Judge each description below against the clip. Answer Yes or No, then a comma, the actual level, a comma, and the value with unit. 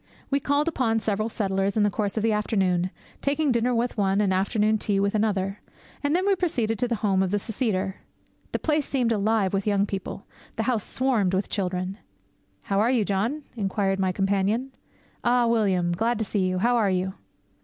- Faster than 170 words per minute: Yes, average, 195 wpm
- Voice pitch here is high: Yes, high, 210 Hz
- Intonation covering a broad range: No, average, 3.4 semitones